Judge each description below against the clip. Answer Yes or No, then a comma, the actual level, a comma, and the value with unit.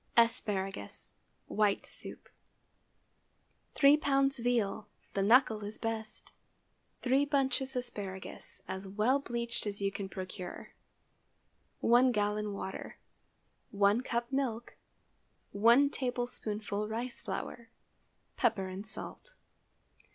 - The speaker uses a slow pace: Yes, slow, 100 wpm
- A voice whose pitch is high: Yes, high, 225 Hz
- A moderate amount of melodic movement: Yes, average, 3.7 semitones